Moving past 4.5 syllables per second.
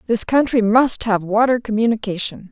Yes: 5.2 syllables/s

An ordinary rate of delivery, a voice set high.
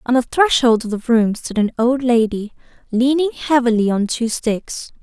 Yes: average, 180 wpm; high, 240 Hz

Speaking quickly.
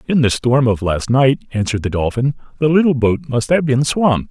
Yes: fast, 225 wpm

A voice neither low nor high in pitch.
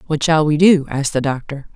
Yes: medium, 150 Hz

